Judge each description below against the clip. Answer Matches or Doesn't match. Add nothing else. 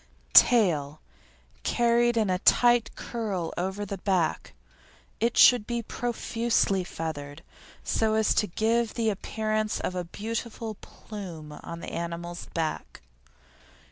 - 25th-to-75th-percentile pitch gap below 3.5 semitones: Doesn't match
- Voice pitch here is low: Doesn't match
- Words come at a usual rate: Doesn't match